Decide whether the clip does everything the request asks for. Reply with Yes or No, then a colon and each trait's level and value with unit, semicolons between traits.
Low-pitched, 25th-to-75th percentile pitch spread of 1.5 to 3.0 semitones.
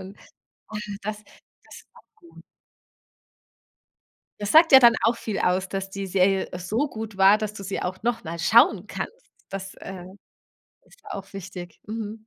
No: high, 200 Hz; average, 2.7 semitones